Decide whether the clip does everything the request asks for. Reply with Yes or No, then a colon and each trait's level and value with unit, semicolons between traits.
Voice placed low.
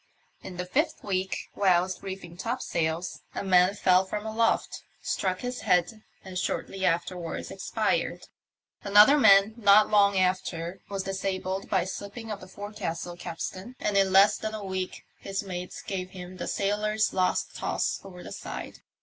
No: high, 190 Hz